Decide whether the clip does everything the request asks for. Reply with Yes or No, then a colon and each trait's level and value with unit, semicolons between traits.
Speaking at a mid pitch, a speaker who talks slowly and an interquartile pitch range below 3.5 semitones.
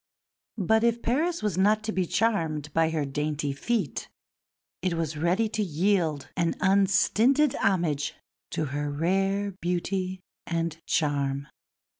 No: medium, 180 Hz; slow, 130 wpm; average, 5.2 semitones